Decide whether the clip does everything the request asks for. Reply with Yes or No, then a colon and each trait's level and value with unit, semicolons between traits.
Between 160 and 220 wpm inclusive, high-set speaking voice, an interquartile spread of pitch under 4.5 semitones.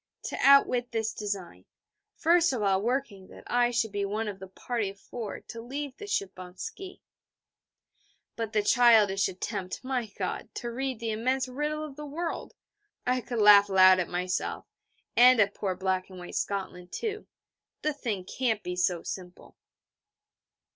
No: average, 170 wpm; high, 220 Hz; average, 5.0 semitones